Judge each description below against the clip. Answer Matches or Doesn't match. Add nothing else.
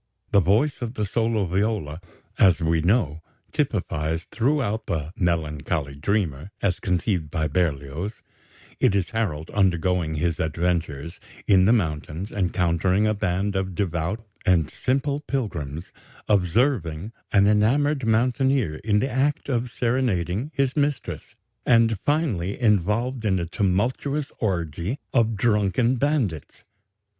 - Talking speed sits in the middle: Doesn't match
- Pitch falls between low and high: Doesn't match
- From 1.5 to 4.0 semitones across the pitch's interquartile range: Doesn't match